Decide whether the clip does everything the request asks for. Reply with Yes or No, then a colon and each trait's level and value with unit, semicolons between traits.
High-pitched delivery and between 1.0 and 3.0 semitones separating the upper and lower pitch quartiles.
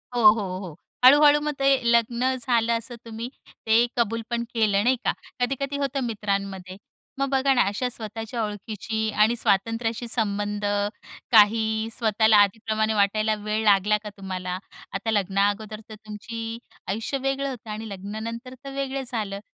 Yes: high, 220 Hz; narrow, 2.6 semitones